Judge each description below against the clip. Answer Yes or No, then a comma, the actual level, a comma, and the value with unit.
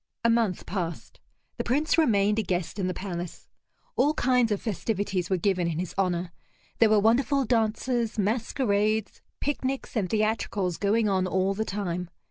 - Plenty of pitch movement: No, average, 3.8 semitones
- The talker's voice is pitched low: No, high, 205 Hz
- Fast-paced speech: No, average, 160 wpm